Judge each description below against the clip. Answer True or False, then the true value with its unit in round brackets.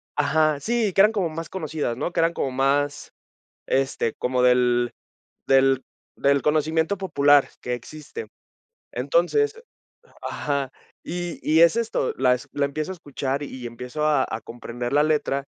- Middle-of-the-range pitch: True (145 Hz)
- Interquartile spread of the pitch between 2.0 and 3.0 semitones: False (3.9 semitones)